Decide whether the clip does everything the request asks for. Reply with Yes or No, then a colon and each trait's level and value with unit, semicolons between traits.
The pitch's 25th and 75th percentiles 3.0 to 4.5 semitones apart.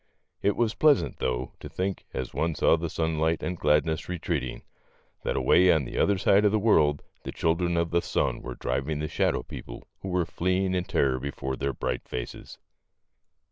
No: average, 5.0 semitones